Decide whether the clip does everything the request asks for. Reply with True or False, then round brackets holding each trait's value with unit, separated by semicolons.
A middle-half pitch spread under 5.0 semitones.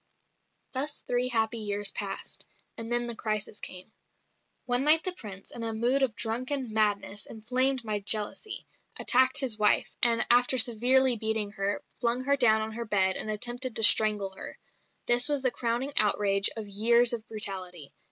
True (3.0 semitones)